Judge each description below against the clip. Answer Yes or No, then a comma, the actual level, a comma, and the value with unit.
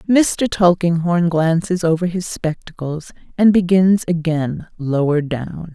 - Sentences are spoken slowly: Yes, slow, 115 wpm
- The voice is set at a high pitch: No, medium, 170 Hz